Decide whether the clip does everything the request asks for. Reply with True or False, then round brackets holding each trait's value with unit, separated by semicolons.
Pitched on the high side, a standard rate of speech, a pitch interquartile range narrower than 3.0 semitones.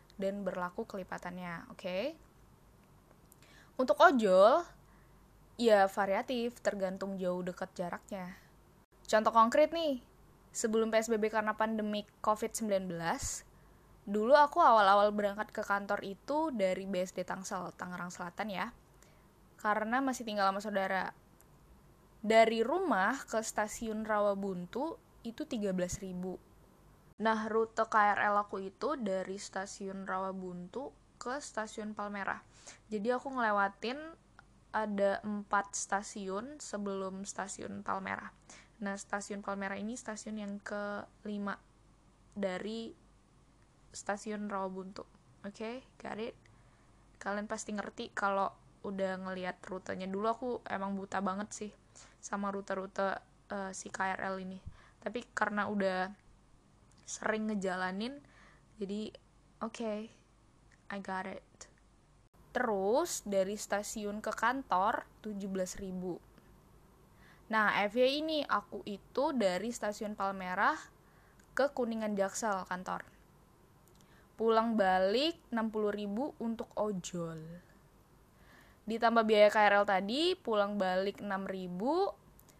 True (205 Hz; 100 wpm; 2.6 semitones)